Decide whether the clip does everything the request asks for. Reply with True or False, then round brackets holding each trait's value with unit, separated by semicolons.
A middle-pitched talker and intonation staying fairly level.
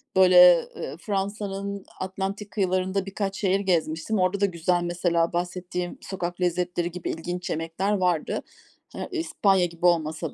True (180 Hz; 2.0 semitones)